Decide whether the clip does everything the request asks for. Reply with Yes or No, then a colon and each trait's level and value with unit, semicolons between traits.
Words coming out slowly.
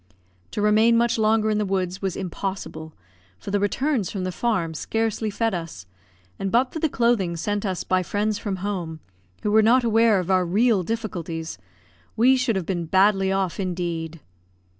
No: average, 180 wpm